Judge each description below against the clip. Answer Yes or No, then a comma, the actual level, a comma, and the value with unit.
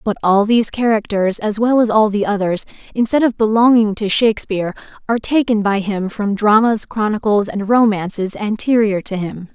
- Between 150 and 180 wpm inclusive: Yes, average, 170 wpm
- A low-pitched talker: No, high, 210 Hz